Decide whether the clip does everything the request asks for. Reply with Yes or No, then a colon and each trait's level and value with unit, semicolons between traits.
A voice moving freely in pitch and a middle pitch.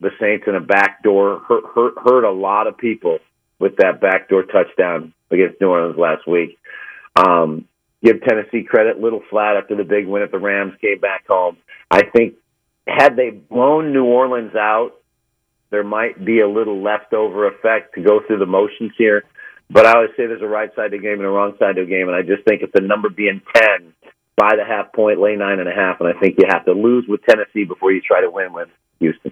No: wide, 5.9 semitones; low, 105 Hz